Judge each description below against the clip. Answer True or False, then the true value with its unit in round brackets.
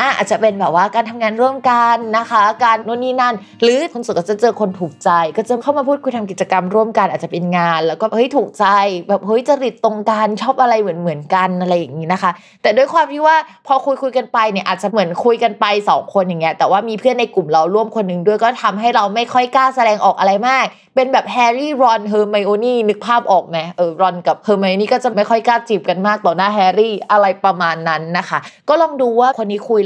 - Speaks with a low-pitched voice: False (215 Hz)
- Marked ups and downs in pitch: False (4.2 semitones)